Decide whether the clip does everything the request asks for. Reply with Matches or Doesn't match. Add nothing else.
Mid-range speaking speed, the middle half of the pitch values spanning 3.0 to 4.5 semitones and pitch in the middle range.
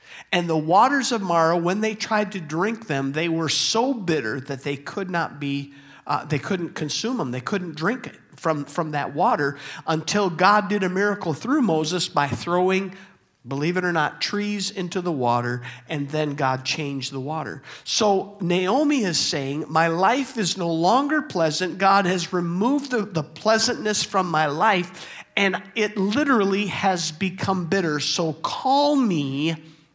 Doesn't match